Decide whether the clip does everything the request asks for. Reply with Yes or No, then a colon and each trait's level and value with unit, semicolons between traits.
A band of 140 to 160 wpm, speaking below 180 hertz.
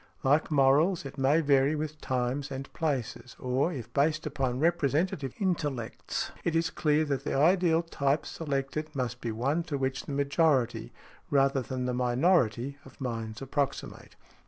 Yes: average, 155 wpm; medium, 140 Hz